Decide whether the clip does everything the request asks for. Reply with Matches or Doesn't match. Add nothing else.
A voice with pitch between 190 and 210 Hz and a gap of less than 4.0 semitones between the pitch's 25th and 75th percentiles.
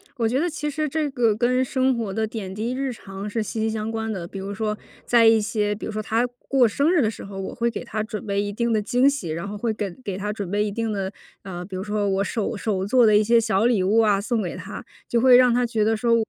Doesn't match